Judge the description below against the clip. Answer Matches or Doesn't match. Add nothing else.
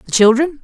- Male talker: Doesn't match